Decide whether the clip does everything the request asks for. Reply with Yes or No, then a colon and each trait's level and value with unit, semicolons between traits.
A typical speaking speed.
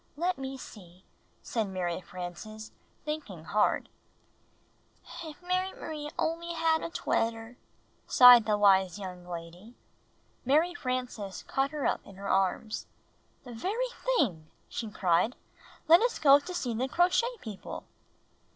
No: slow, 130 wpm